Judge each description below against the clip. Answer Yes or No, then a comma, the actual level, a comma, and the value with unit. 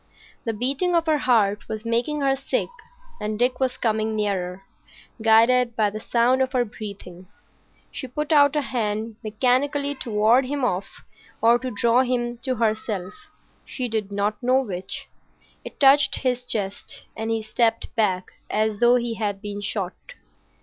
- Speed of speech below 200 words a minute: Yes, average, 165 wpm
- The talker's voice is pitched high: Yes, high, 230 Hz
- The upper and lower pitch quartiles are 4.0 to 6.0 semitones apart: No, average, 3.4 semitones